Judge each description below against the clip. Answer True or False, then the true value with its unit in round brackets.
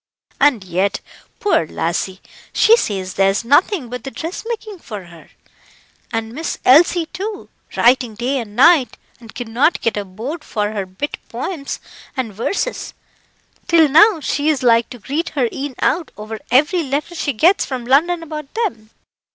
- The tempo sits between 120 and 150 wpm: False (160 wpm)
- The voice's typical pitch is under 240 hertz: False (260 Hz)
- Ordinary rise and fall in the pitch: False (6.8 semitones)